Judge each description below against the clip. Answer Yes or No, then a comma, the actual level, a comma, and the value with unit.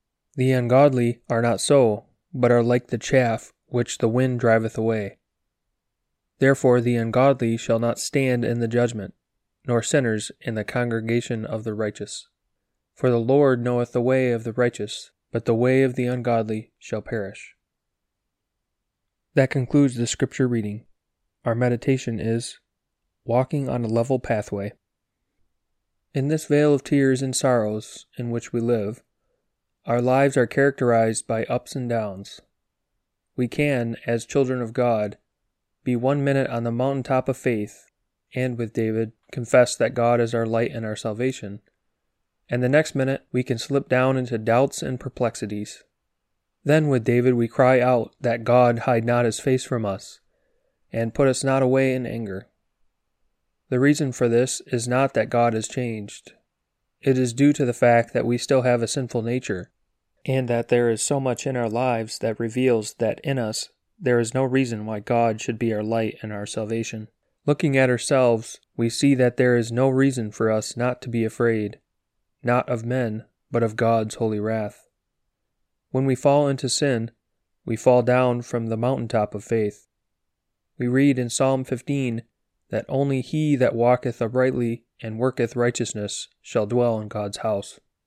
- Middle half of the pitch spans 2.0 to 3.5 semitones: Yes, narrow, 2.4 semitones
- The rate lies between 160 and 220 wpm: Yes, average, 170 wpm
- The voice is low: Yes, low, 120 Hz